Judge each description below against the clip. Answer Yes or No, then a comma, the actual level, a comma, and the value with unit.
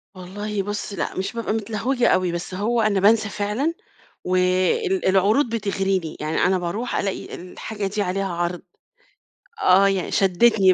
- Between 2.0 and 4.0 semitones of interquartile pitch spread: Yes, average, 2.9 semitones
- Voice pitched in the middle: No, high, 195 Hz